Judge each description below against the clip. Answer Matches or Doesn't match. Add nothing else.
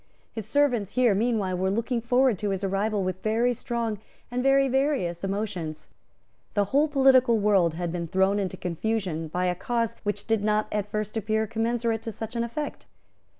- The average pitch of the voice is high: Matches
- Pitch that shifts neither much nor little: Matches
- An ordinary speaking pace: Matches